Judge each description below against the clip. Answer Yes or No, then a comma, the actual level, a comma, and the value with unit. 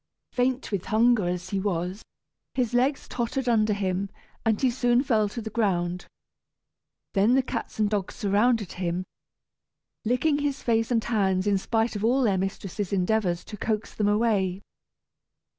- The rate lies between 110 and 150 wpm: No, average, 160 wpm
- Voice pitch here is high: Yes, high, 215 Hz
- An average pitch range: Yes, average, 3.8 semitones